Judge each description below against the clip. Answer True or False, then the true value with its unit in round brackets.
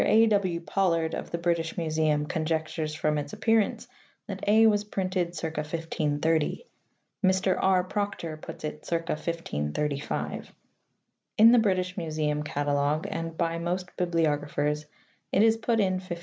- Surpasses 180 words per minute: False (140 wpm)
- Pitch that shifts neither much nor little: True (3.6 semitones)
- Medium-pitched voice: True (165 Hz)